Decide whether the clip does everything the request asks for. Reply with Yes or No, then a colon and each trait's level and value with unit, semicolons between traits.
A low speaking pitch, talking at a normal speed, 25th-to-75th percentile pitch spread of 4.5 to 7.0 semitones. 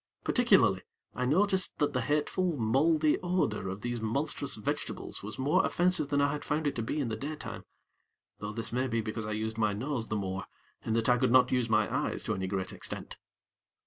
No: low, 125 Hz; fast, 210 wpm; average, 5.2 semitones